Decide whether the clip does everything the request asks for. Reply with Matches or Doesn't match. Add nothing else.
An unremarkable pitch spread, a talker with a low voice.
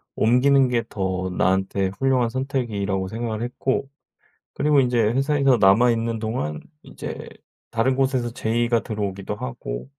Matches